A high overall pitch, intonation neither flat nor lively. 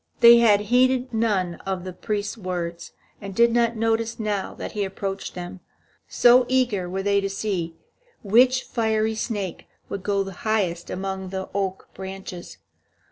Yes: high, 200 Hz; average, 3.1 semitones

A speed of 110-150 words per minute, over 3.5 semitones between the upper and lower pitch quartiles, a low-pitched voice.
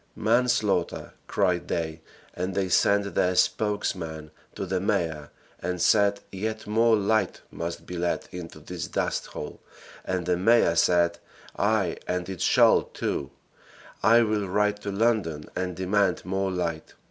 No: average, 140 wpm; average, 3.1 semitones; very low, 95 Hz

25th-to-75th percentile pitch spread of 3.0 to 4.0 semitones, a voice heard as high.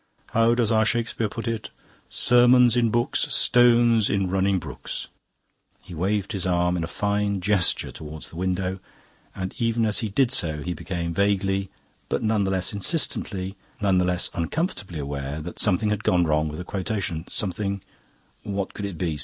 No: average, 3.7 semitones; low, 100 Hz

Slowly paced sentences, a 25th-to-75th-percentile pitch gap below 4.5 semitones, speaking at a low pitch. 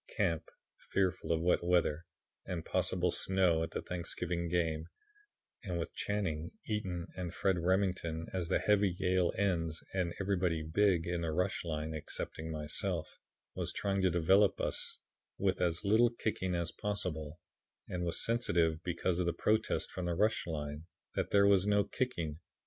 No: average, 160 wpm; average, 2.8 semitones; very low, 90 Hz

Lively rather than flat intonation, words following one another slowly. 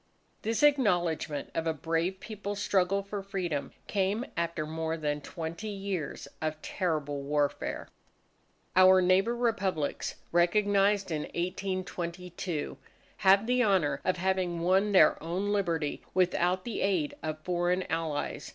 No: average, 3.4 semitones; slow, 125 wpm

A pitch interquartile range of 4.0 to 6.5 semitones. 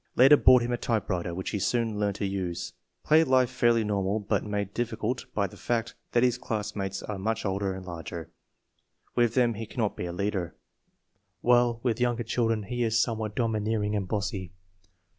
No: average, 3.2 semitones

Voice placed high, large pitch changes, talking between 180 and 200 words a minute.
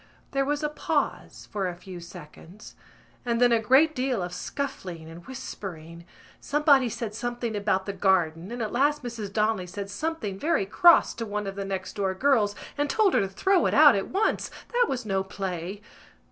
Yes: high, 210 Hz; wide, 6.0 semitones; average, 190 wpm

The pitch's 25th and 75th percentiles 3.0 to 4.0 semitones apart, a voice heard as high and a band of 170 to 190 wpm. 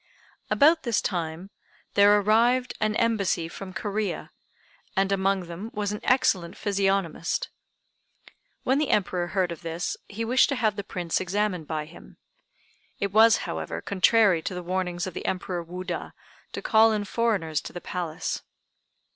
No: average, 3.6 semitones; high, 195 Hz; average, 155 wpm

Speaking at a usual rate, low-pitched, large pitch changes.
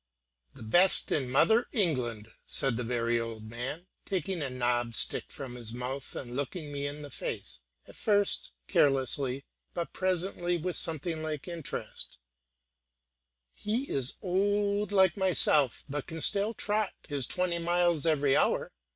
No: average, 145 wpm; medium, 150 Hz; wide, 6.2 semitones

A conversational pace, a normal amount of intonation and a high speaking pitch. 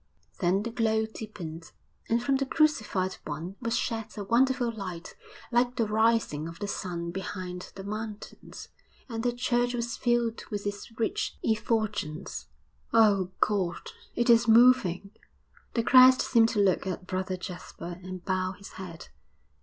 Yes: average, 150 wpm; average, 4.0 semitones; high, 210 Hz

